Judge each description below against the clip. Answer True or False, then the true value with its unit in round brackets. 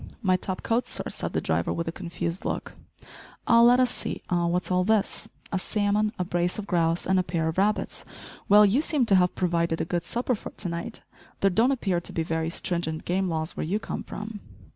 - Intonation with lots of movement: False (3.8 semitones)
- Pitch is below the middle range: False (185 Hz)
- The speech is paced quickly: True (225 wpm)